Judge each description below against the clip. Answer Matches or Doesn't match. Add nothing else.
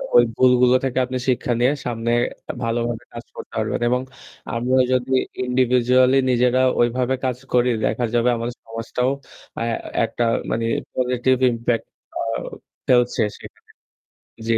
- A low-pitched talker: Matches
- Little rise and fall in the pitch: Matches